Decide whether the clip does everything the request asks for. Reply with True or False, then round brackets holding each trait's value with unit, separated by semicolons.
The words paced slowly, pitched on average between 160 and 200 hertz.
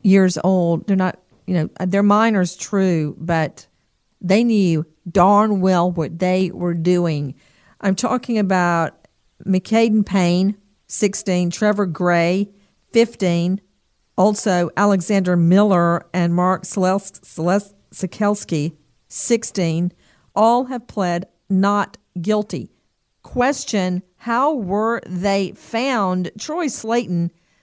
True (105 wpm; 190 Hz)